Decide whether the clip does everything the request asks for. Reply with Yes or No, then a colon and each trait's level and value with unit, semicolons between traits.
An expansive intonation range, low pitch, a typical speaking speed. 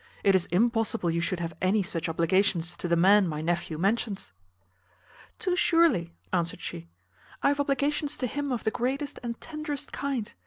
No: wide, 8.3 semitones; high, 205 Hz; average, 170 wpm